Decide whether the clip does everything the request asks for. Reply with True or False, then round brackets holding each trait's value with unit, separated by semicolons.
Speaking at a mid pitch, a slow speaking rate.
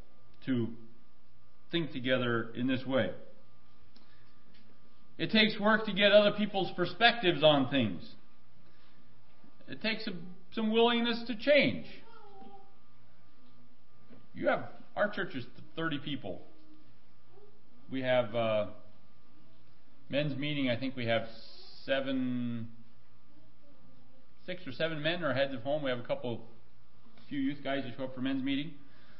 False (130 Hz; 125 wpm)